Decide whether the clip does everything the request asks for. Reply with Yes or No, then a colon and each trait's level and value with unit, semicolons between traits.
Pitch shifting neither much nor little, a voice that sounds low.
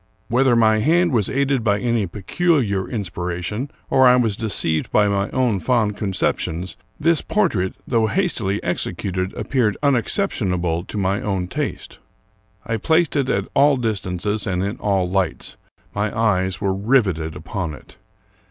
Yes: average, 5.0 semitones; low, 105 Hz